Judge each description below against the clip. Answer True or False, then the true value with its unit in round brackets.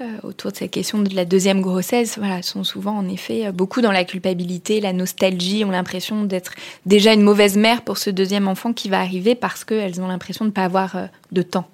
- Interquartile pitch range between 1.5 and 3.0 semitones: True (2.4 semitones)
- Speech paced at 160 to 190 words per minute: False (220 wpm)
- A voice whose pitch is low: False (195 Hz)